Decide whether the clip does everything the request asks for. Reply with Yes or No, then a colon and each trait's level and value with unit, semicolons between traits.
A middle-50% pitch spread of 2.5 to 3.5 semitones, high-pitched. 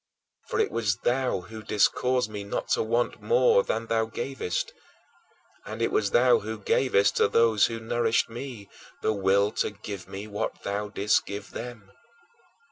No: average, 2.8 semitones; low, 110 Hz